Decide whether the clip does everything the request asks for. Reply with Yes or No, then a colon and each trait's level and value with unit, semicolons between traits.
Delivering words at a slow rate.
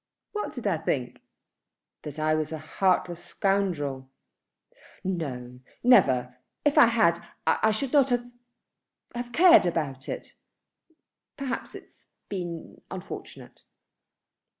Yes: slow, 115 wpm